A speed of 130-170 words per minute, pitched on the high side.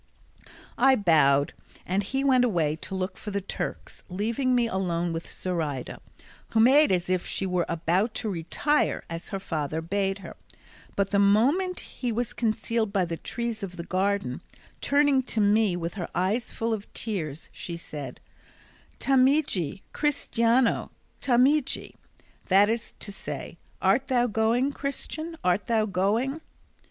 Yes: average, 150 wpm; high, 205 Hz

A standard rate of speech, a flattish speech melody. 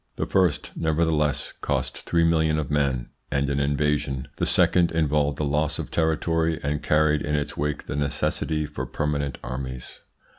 Yes: average, 160 wpm; narrow, 1.9 semitones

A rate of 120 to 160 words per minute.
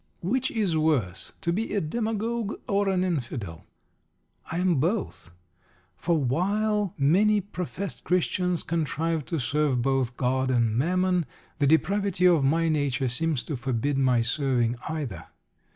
Yes: slow, 135 wpm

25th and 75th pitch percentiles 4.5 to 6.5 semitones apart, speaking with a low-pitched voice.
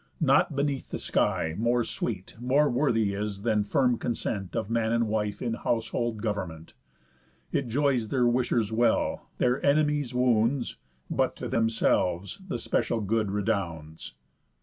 No: average, 3.3 semitones; low, 115 Hz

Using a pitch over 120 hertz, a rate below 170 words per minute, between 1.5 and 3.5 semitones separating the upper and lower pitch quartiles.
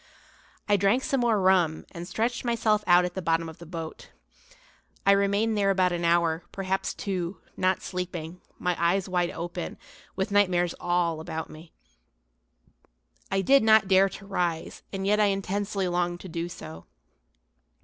Yes: medium, 185 Hz; average, 160 wpm; narrow, 2.6 semitones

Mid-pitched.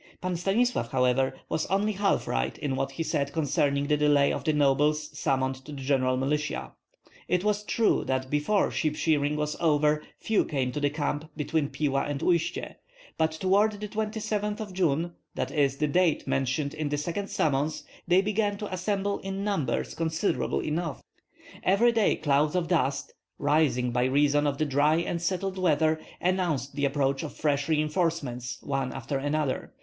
Yes: medium, 150 Hz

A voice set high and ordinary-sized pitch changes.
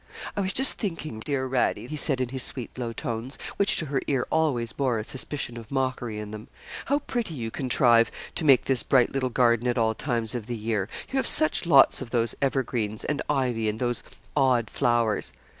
No: low, 125 Hz; average, 3.2 semitones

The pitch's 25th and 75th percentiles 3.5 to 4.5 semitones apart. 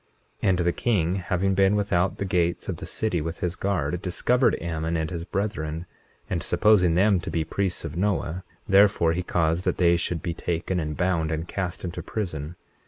No: average, 2.8 semitones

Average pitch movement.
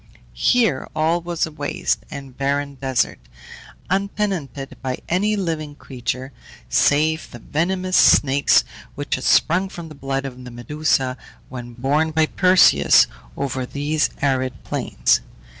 Yes: average, 3.9 semitones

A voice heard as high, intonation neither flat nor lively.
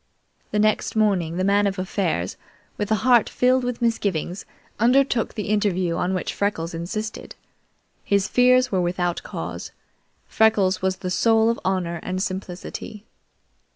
Yes: high, 200 Hz; average, 3.2 semitones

